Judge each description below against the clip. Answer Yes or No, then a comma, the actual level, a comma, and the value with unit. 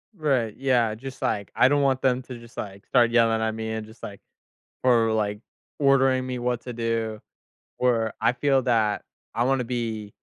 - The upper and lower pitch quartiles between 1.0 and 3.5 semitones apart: Yes, narrow, 2.5 semitones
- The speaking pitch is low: Yes, low, 120 Hz